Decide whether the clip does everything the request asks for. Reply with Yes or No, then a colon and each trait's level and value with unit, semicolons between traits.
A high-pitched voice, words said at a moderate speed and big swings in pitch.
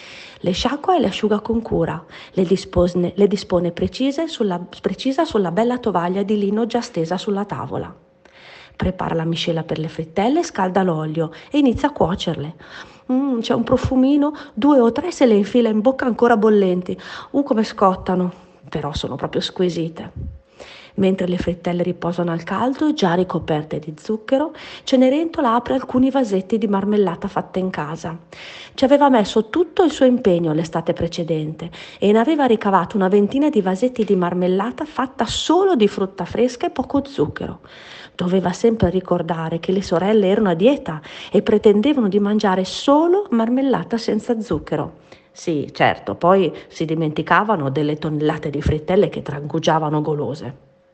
Yes: high, 200 Hz; average, 155 wpm; wide, 5.9 semitones